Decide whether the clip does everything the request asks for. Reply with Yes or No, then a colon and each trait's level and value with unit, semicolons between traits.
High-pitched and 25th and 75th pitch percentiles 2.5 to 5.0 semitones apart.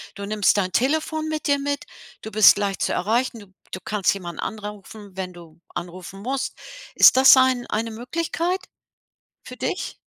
No: high, 215 Hz; wide, 5.5 semitones